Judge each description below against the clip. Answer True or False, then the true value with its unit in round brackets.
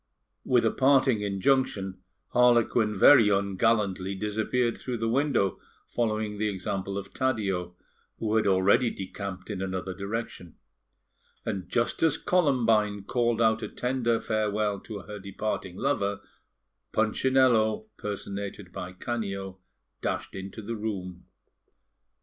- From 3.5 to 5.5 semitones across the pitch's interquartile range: False (3.1 semitones)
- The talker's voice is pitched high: False (105 Hz)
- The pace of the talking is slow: True (120 wpm)